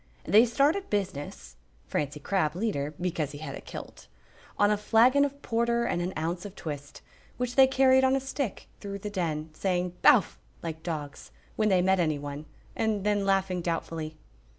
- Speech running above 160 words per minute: Yes, average, 175 wpm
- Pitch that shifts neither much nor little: No, wide, 6.3 semitones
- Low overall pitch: No, high, 190 Hz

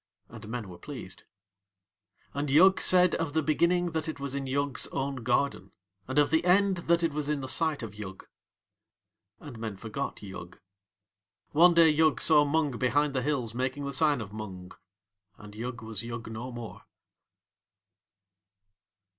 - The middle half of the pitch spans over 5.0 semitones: Yes, wide, 5.4 semitones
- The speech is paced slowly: No, average, 165 wpm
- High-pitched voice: No, medium, 140 Hz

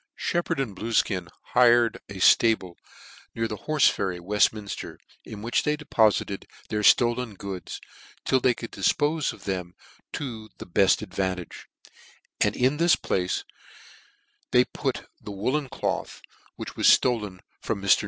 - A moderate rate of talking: Yes, average, 145 wpm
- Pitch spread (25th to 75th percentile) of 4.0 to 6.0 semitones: Yes, average, 4.5 semitones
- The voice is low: Yes, low, 110 Hz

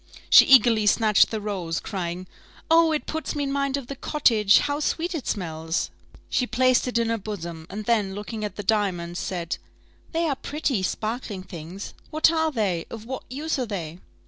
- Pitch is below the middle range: No, high, 220 Hz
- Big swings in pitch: Yes, wide, 6.6 semitones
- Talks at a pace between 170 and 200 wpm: Yes, average, 190 wpm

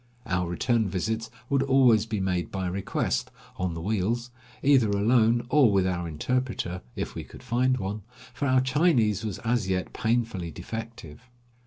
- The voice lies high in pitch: No, low, 110 Hz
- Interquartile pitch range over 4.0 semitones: Yes, average, 4.8 semitones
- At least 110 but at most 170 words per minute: Yes, average, 160 wpm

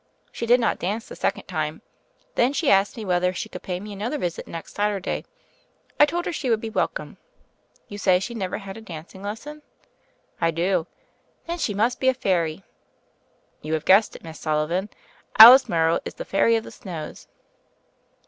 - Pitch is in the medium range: No, high, 200 Hz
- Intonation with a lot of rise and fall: No, average, 4.6 semitones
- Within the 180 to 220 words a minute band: Yes, average, 185 wpm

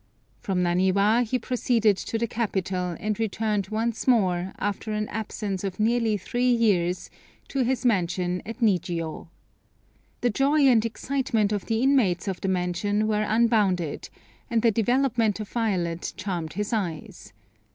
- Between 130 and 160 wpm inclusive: Yes, average, 145 wpm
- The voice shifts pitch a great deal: No, average, 3.8 semitones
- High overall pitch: Yes, high, 210 Hz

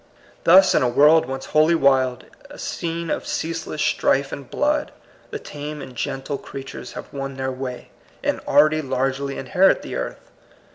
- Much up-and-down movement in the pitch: No, average, 3.6 semitones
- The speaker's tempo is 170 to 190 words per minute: No, average, 160 wpm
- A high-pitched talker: No, medium, 140 Hz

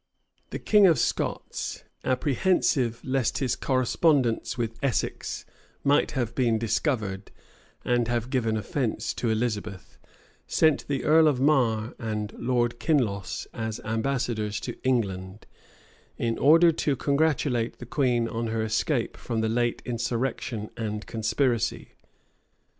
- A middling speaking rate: No, slow, 125 wpm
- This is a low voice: Yes, low, 120 Hz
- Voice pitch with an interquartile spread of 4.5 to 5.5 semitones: No, average, 3.4 semitones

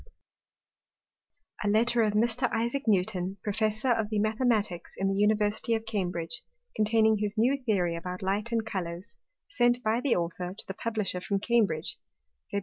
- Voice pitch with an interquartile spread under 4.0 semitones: Yes, average, 3.0 semitones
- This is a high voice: Yes, high, 215 Hz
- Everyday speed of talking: Yes, average, 160 wpm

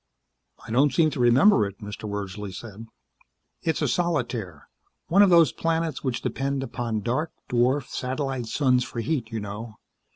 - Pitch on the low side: Yes, low, 125 Hz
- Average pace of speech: Yes, average, 160 wpm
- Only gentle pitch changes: No, average, 5.1 semitones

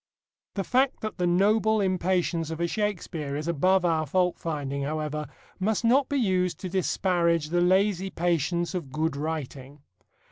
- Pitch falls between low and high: Yes, medium, 175 Hz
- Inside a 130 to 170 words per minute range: Yes, average, 155 wpm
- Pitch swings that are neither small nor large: Yes, average, 3.5 semitones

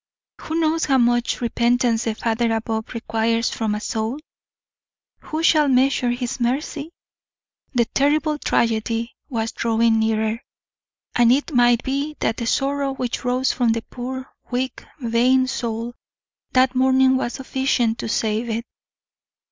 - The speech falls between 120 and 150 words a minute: Yes, average, 140 wpm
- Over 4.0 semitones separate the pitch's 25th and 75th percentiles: No, narrow, 2.5 semitones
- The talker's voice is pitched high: Yes, high, 245 Hz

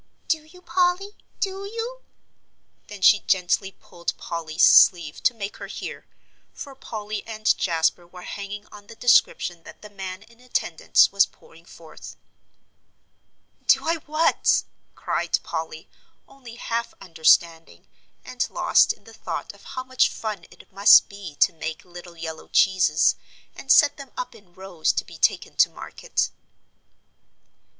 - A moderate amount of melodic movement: No, wide, 6.9 semitones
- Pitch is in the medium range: No, high, 200 Hz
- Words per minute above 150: No, average, 145 wpm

